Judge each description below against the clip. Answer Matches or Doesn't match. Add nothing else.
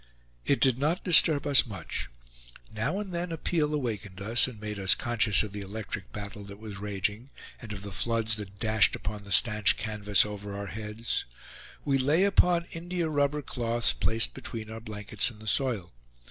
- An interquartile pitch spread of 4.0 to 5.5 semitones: Matches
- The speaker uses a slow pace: Doesn't match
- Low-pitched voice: Matches